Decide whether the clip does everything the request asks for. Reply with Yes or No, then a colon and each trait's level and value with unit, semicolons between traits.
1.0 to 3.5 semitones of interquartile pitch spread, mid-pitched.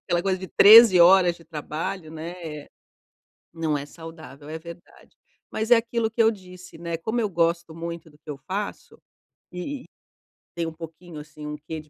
Yes: average, 3.0 semitones; medium, 170 Hz